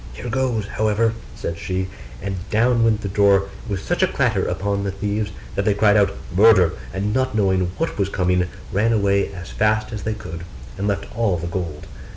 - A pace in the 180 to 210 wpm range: Yes, average, 195 wpm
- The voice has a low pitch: Yes, low, 100 Hz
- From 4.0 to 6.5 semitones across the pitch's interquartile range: No, narrow, 2.4 semitones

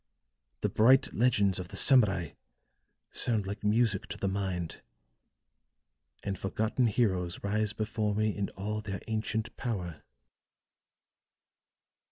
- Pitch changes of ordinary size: No, narrow, 2.3 semitones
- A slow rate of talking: Yes, slow, 115 wpm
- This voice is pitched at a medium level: No, low, 105 Hz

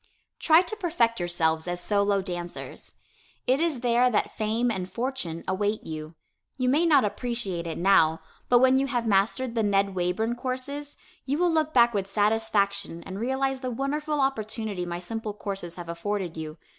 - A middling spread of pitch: No, wide, 5.7 semitones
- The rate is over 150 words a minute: Yes, average, 170 wpm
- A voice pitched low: No, high, 220 Hz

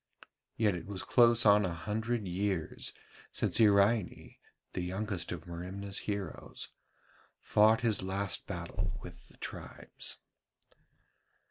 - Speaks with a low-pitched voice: Yes, low, 100 Hz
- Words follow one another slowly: Yes, slow, 115 wpm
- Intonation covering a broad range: No, average, 2.7 semitones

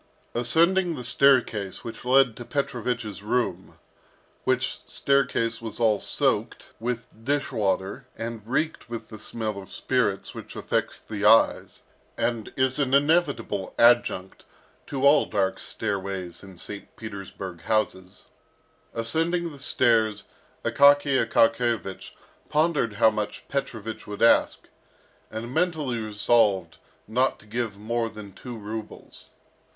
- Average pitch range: Yes, average, 4.0 semitones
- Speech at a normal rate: No, slow, 125 wpm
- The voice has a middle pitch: No, low, 115 Hz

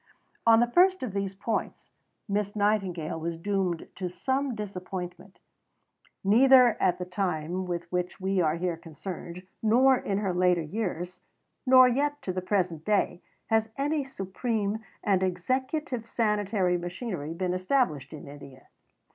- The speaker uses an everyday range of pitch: Yes, average, 4.2 semitones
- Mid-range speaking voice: No, high, 195 Hz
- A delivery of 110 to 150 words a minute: Yes, average, 140 wpm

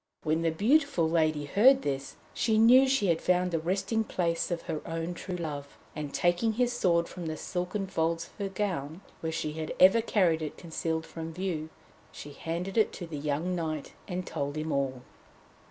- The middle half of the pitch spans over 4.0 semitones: No, average, 3.5 semitones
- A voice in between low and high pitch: Yes, medium, 170 Hz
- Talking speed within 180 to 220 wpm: Yes, average, 190 wpm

